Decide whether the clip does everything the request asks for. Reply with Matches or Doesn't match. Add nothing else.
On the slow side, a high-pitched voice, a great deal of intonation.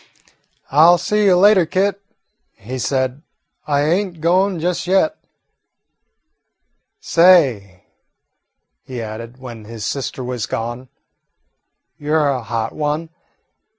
Doesn't match